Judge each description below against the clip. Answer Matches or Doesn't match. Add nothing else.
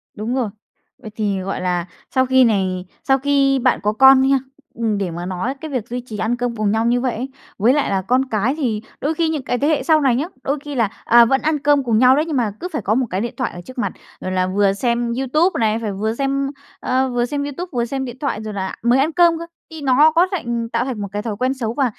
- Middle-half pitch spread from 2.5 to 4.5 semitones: Matches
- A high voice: Matches